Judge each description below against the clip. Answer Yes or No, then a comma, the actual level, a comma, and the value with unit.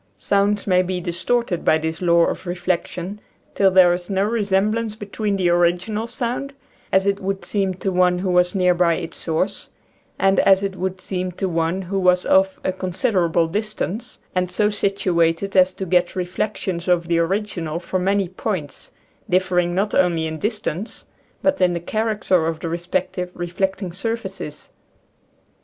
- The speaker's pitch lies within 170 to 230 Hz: Yes, medium, 185 Hz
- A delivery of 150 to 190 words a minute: Yes, average, 170 wpm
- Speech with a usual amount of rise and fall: No, narrow, 2.2 semitones